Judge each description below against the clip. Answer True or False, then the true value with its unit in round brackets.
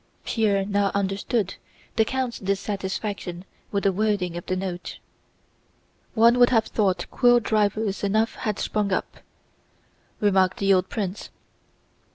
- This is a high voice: True (200 Hz)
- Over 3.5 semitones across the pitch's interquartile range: False (2.4 semitones)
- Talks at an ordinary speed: False (130 wpm)